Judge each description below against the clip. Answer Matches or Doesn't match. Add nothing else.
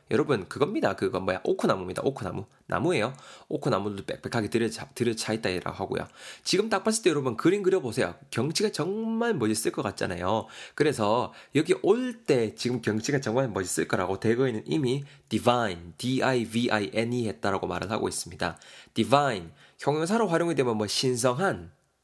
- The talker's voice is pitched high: Doesn't match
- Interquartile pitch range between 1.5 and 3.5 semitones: Doesn't match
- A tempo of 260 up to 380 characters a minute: Doesn't match